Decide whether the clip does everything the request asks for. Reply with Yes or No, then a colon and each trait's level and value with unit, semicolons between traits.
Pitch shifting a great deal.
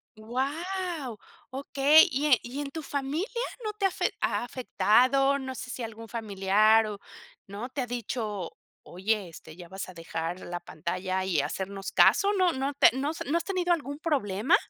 Yes: wide, 6.5 semitones